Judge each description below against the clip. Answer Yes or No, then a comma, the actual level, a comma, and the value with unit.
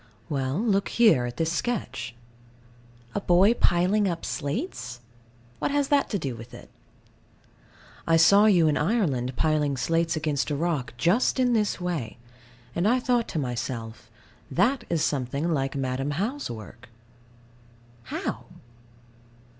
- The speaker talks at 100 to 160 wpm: Yes, average, 140 wpm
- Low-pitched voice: No, medium, 165 Hz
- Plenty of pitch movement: Yes, wide, 7.6 semitones